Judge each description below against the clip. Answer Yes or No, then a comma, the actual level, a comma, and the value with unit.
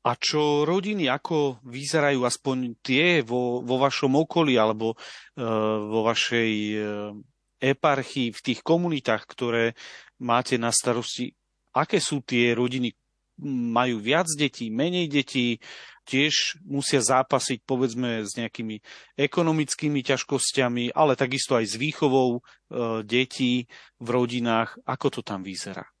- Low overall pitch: Yes, low, 125 Hz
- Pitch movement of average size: Yes, average, 3.2 semitones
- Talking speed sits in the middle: Yes, average, 120 wpm